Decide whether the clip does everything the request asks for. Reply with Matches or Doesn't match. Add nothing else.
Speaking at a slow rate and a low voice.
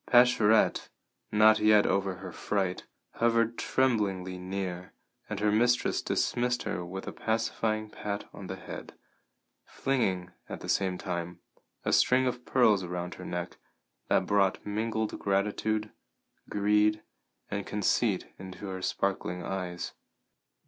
Matches